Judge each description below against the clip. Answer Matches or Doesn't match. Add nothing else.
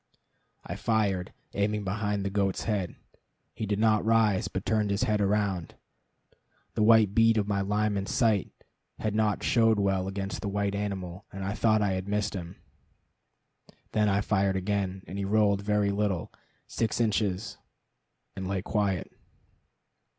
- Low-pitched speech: Matches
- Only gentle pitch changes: Matches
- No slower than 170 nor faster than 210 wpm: Doesn't match